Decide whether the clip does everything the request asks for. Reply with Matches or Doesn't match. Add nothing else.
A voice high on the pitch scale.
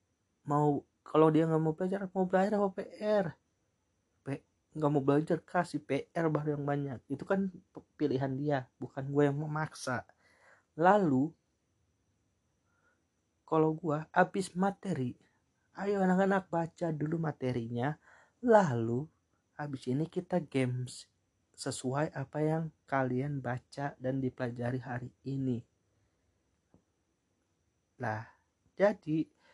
Doesn't match